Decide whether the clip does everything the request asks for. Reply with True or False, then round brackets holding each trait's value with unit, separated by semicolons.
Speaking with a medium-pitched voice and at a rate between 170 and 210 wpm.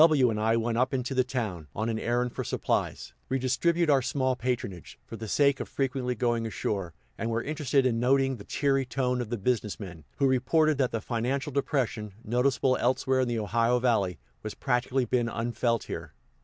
False (125 Hz; 195 wpm)